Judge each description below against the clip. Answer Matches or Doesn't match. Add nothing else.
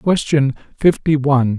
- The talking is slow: Matches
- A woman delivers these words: Doesn't match